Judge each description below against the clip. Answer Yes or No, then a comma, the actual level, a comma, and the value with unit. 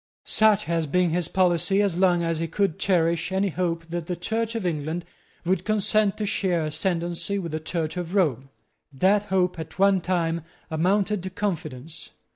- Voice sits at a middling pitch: Yes, medium, 175 Hz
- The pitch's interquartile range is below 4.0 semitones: Yes, average, 3.0 semitones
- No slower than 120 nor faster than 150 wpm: No, average, 175 wpm